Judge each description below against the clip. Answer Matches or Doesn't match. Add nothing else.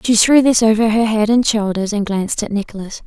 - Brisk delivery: Matches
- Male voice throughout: Doesn't match